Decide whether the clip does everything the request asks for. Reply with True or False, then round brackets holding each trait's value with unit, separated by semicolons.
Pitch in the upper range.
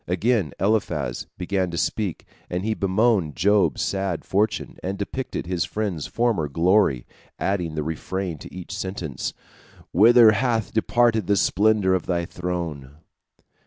False (95 Hz)